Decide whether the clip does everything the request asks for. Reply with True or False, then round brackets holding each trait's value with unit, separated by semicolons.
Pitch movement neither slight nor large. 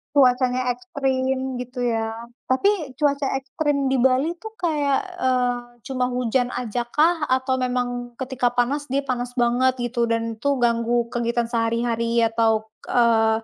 False (1.9 semitones)